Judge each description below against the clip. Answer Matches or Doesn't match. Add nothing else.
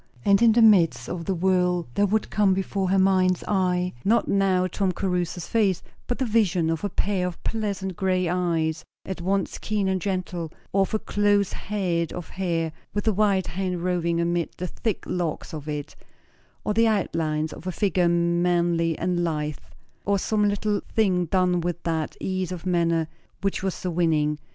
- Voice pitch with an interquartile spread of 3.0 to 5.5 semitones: Doesn't match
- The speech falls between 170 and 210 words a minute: Matches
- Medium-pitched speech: Matches